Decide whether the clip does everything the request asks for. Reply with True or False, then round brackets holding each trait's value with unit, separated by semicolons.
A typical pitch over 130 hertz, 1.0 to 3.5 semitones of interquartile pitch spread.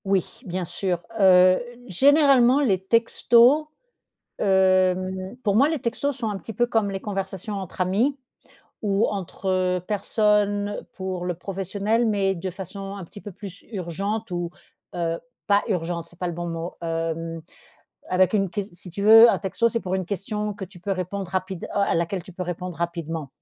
True (190 Hz; 2.7 semitones)